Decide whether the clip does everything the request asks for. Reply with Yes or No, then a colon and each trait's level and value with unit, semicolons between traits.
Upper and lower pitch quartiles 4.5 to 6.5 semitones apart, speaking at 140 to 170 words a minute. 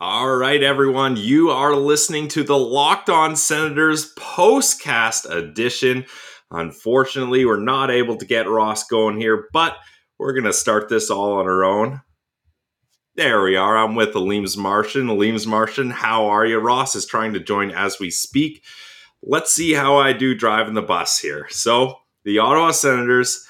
Yes: average, 5.2 semitones; average, 165 wpm